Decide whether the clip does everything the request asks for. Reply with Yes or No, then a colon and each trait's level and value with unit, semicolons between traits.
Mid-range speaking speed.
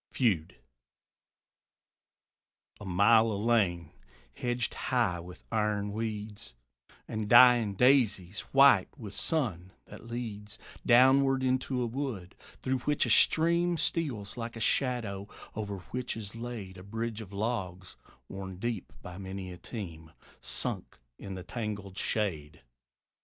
No: slow, 125 wpm